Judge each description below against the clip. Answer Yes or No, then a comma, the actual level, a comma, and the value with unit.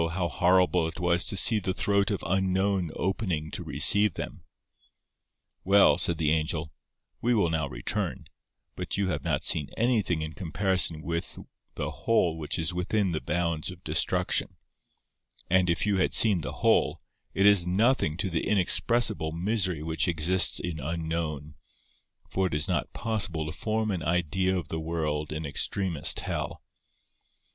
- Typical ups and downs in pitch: Yes, average, 3.4 semitones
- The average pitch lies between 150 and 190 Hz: No, very low, 90 Hz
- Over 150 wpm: Yes, average, 160 wpm